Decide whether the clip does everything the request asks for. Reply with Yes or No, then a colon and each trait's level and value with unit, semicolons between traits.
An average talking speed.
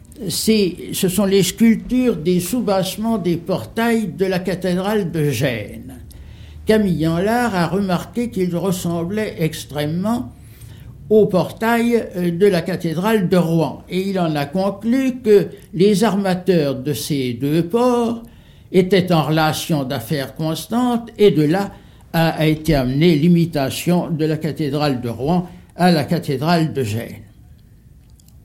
No: slow, 130 wpm